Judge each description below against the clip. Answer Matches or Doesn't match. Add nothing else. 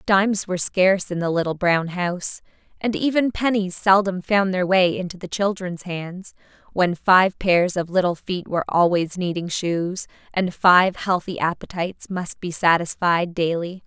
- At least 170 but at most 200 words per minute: Doesn't match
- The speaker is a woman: Matches